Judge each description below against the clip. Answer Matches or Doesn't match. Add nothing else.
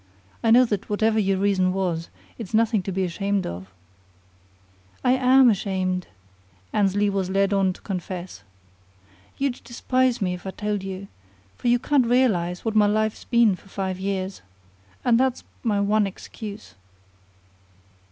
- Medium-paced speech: Matches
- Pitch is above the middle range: Matches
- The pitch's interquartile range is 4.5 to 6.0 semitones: Doesn't match